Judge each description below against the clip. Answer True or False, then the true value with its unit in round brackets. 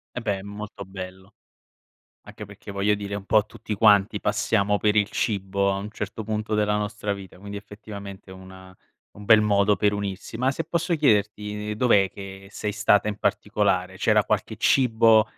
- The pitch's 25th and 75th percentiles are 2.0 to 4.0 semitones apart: False (1.4 semitones)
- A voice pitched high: False (105 Hz)